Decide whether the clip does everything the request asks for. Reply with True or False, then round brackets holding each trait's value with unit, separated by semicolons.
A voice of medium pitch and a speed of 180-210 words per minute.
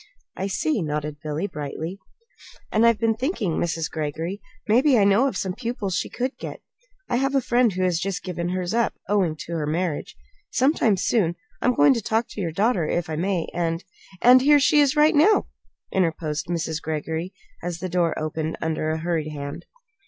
True (180 Hz; 195 wpm)